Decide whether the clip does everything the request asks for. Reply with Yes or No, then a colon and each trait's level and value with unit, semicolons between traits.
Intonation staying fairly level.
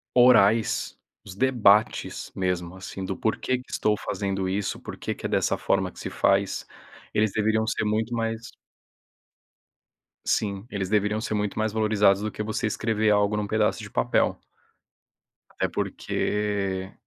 Yes: narrow, 1.9 semitones